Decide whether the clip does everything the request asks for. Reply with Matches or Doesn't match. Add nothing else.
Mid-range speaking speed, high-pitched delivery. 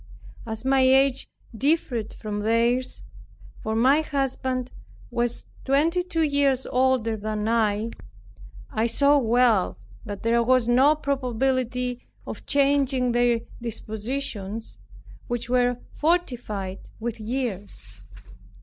Doesn't match